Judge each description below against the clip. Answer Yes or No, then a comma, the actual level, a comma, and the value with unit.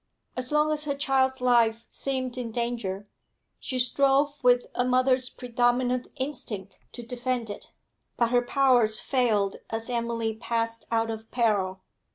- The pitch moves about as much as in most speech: No, narrow, 2.1 semitones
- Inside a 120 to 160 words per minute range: Yes, average, 145 wpm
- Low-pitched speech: No, high, 245 Hz